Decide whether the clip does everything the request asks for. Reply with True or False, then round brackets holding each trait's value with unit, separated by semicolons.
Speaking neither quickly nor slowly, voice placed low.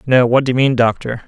False (285 wpm; 125 Hz)